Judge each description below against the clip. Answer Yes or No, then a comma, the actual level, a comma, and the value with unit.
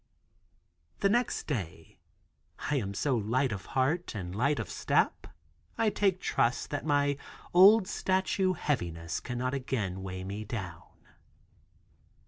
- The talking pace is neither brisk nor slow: No, slow, 125 wpm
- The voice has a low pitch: Yes, low, 130 Hz